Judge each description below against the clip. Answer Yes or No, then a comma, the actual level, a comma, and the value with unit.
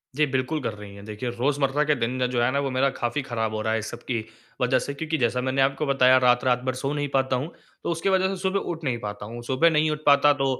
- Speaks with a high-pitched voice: No, low, 130 Hz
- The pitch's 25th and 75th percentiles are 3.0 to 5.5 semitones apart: Yes, average, 3.5 semitones